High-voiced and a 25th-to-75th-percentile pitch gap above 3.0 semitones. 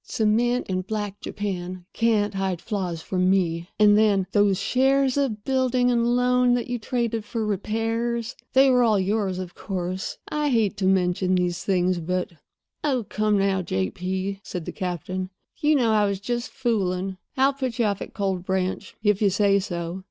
Yes: high, 205 Hz; average, 4.2 semitones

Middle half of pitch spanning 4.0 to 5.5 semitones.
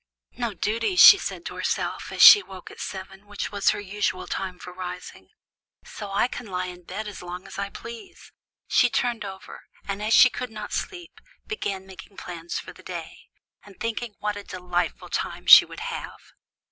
No: average, 3.5 semitones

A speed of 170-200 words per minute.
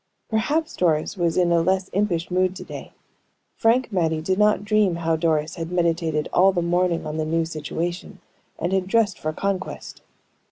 Yes: average, 175 wpm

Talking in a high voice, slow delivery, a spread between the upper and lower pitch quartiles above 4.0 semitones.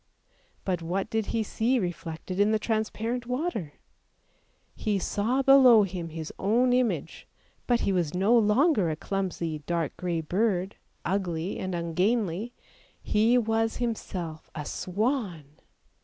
Yes: high, 200 Hz; slow, 130 wpm; average, 4.9 semitones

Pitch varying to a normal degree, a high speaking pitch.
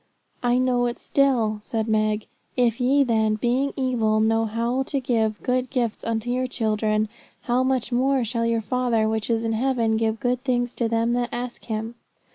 No: narrow, 2.2 semitones; high, 235 Hz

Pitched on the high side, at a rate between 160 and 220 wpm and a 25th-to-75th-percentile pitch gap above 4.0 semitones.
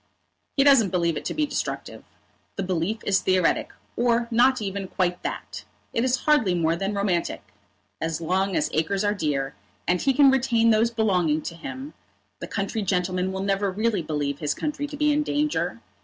Yes: high, 195 Hz; average, 185 wpm; average, 5.2 semitones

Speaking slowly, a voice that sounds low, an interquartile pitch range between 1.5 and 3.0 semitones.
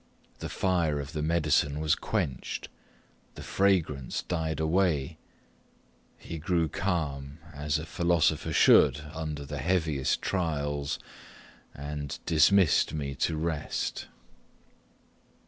Yes: slow, 105 wpm; very low, 75 Hz; average, 2.7 semitones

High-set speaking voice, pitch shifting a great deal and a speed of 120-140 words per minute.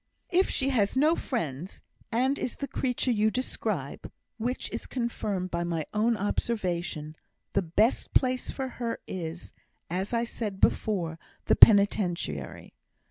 Yes: high, 210 Hz; wide, 6.0 semitones; slow, 135 wpm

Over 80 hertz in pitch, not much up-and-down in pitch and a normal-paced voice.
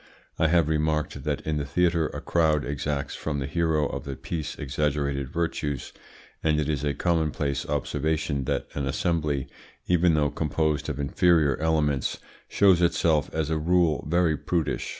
No: very low, 75 Hz; narrow, 2.2 semitones; average, 160 wpm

